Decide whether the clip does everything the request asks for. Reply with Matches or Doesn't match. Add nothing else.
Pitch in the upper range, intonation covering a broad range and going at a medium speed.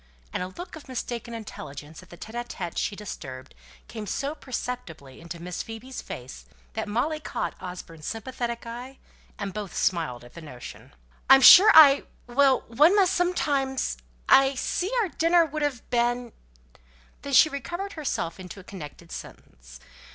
Matches